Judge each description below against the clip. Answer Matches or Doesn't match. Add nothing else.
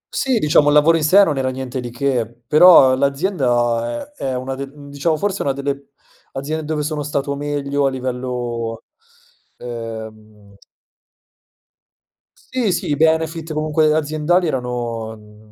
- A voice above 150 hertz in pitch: Doesn't match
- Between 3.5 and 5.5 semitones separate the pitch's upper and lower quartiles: Matches